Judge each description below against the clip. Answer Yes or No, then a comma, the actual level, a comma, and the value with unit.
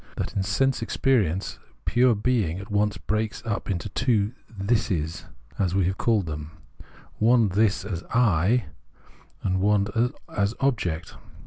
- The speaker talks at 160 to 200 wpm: No, average, 150 wpm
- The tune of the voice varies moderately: Yes, average, 3.7 semitones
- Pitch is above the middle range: No, low, 105 Hz